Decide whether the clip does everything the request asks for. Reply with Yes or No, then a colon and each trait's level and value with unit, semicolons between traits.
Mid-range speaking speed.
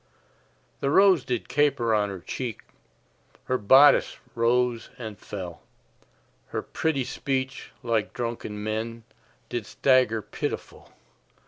No: slow, 110 wpm